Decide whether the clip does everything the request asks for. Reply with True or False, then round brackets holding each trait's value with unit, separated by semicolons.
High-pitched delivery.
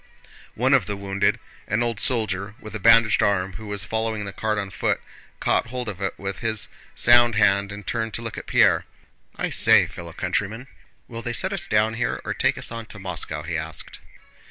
False (105 Hz)